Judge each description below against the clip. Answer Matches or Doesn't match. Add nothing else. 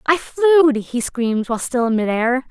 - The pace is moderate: Matches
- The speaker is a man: Doesn't match